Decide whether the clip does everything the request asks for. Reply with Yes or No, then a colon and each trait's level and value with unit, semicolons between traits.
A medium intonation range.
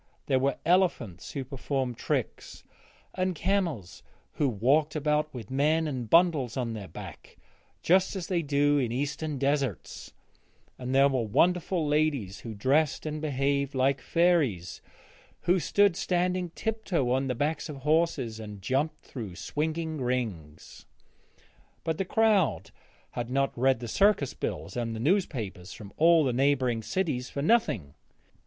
Yes: average, 5.0 semitones